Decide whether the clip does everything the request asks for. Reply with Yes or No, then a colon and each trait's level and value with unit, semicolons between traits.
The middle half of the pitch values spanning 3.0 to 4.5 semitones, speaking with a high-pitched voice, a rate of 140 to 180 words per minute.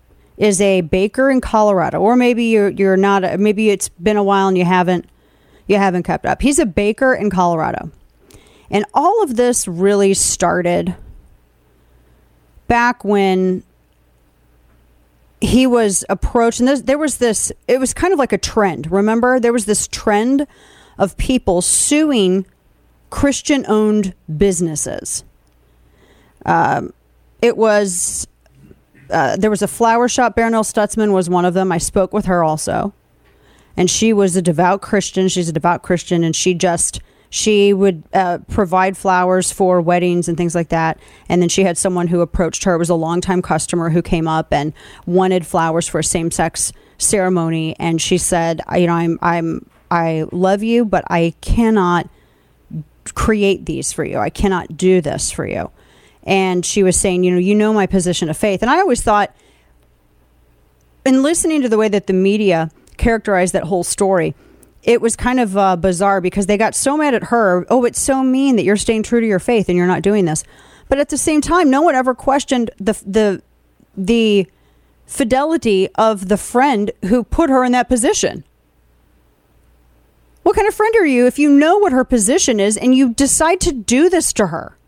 No: average, 5.1 semitones; high, 195 Hz; average, 175 wpm